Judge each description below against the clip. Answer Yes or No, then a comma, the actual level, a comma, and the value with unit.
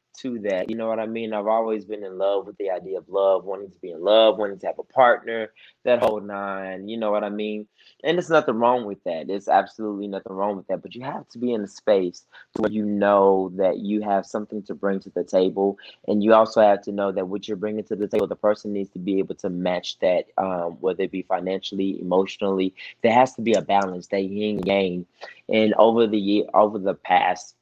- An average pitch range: No, narrow, 1.9 semitones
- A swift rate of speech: Yes, fast, 245 wpm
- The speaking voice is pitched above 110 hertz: No, low, 100 Hz